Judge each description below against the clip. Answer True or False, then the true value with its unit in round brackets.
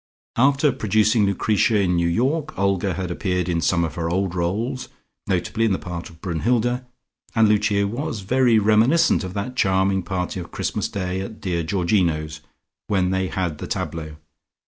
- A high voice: False (95 Hz)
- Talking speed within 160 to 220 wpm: True (170 wpm)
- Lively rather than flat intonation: False (3.8 semitones)